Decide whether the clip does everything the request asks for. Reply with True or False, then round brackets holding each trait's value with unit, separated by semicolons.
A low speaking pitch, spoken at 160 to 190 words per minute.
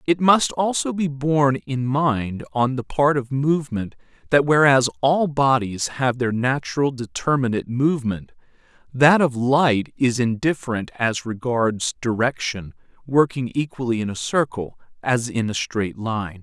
False (130 Hz; 145 wpm)